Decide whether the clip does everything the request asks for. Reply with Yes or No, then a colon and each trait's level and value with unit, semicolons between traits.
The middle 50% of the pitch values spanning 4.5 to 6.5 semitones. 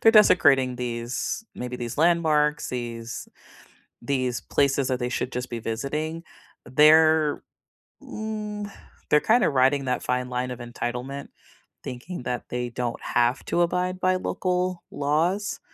Yes: wide, 5.5 semitones